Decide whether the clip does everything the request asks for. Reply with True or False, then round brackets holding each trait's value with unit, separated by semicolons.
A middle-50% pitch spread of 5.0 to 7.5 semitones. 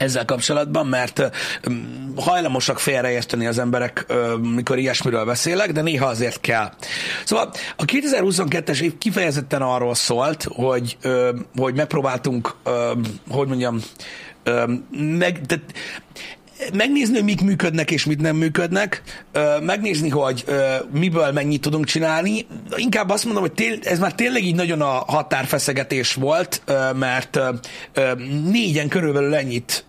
True (5.5 semitones)